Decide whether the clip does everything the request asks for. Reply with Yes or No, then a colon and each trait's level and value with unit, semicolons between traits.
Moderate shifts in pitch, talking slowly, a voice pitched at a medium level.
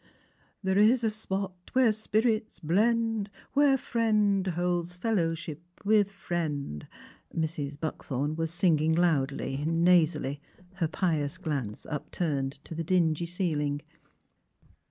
Yes: average, 4.9 semitones; slow, 120 wpm; medium, 175 Hz